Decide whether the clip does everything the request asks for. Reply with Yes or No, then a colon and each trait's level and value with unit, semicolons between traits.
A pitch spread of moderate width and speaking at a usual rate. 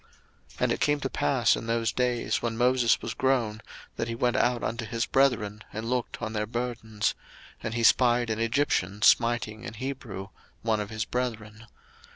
No: narrow, 2.1 semitones; average, 185 wpm